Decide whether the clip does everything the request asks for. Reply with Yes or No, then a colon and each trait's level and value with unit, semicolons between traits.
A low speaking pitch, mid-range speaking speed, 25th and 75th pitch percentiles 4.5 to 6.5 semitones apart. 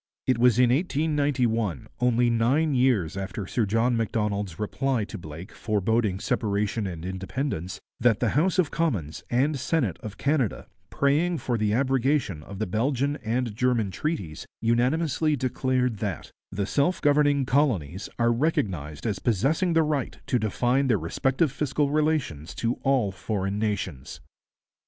Yes: low, 120 Hz; average, 145 wpm; wide, 5.6 semitones